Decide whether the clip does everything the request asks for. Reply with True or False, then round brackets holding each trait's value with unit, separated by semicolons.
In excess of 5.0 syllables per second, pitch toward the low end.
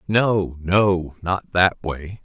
False (2.5 syllables/s; 90 Hz)